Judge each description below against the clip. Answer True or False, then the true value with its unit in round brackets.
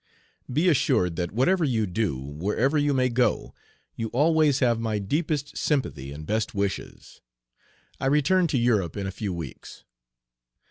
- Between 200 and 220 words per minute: False (150 wpm)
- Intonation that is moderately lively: False (6.9 semitones)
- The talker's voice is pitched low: True (115 Hz)